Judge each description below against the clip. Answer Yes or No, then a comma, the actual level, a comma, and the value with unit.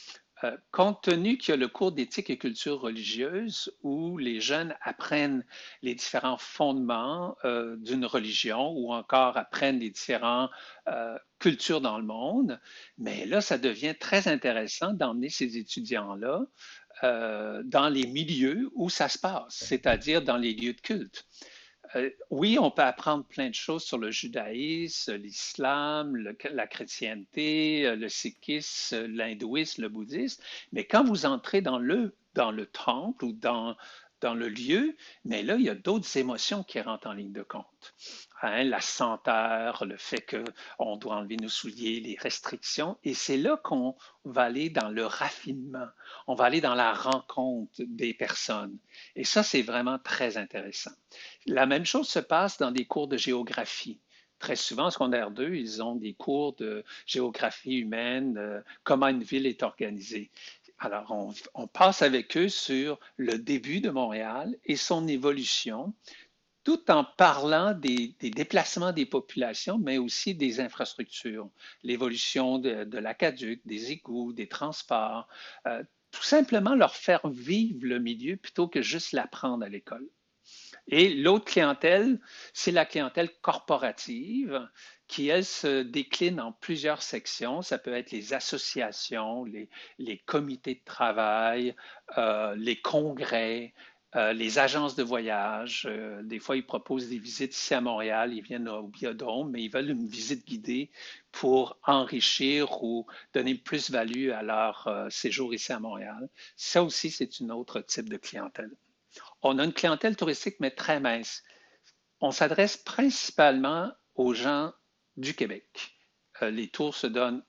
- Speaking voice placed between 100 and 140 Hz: Yes, low, 135 Hz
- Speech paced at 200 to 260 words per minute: No, average, 155 wpm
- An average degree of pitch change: No, wide, 7.2 semitones